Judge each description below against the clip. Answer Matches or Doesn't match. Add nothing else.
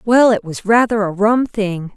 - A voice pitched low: Doesn't match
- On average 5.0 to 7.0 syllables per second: Doesn't match